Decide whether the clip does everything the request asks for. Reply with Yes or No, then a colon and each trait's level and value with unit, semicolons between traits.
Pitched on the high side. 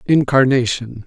No: low, 130 Hz